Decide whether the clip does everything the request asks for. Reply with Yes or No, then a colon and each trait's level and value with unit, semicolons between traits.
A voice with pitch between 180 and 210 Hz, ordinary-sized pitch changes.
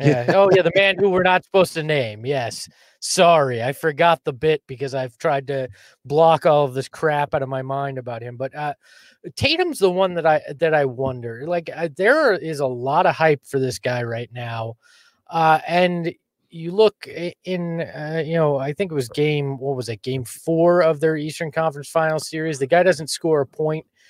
No: medium, 155 Hz; average, 3.8 semitones